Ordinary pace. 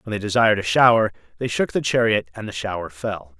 No: fast, 230 wpm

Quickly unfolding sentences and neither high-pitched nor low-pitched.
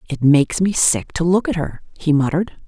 Yes: fast, 225 wpm; medium, 165 Hz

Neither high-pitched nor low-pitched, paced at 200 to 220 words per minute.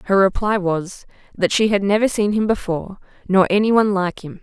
No: high, 200 Hz; fast, 205 wpm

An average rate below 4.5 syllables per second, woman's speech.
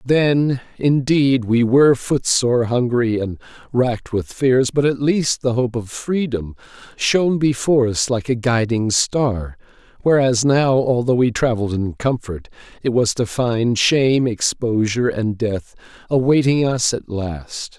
No: 4.2 syllables/s; male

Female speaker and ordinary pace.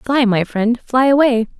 Yes: female; average, 190 wpm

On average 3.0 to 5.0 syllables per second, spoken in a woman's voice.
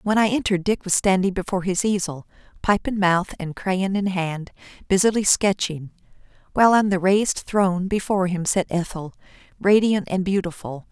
No: 5.3 syllables/s; female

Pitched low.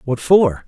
No: medium, 150 Hz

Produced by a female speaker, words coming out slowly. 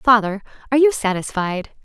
Yes: female; slow, 130 wpm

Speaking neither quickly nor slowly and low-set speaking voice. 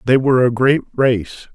Yes: average, 195 wpm; low, 125 Hz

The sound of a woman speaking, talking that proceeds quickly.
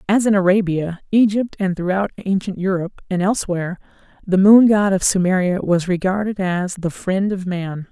No: female; average, 165 wpm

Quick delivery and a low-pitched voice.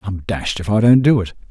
Yes: fast, 280 wpm; low, 105 Hz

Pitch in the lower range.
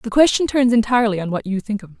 No: high, 225 Hz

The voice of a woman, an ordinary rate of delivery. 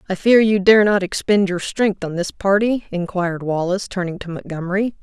Yes: female; average, 190 wpm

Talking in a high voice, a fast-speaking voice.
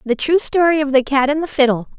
Yes: very high, 280 Hz; fast, 270 wpm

